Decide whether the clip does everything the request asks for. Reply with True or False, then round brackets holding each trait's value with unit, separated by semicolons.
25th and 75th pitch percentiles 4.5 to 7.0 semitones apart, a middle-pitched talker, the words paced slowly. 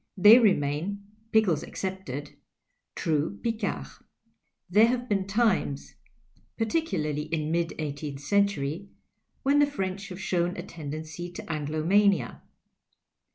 True (5.1 semitones; 175 Hz; 110 wpm)